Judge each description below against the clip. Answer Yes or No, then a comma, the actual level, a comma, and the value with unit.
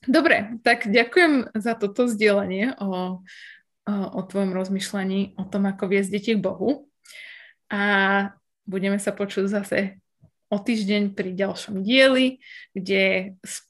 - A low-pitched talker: No, high, 205 Hz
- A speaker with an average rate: Yes, average, 130 wpm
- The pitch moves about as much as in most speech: Yes, average, 3.2 semitones